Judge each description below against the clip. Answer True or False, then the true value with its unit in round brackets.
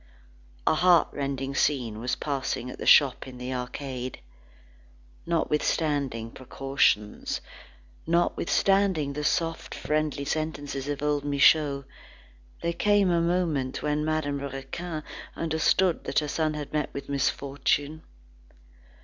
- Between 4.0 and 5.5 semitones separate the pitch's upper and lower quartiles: False (2.7 semitones)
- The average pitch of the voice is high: False (145 Hz)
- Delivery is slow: True (115 wpm)